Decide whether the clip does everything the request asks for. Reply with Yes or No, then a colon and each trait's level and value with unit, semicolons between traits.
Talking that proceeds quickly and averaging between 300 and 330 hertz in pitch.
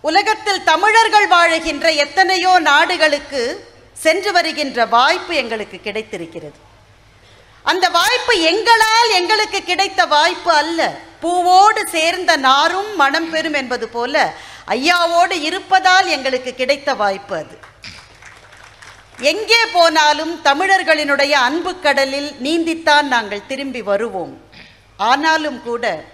No: average, 95 wpm; very high, 315 Hz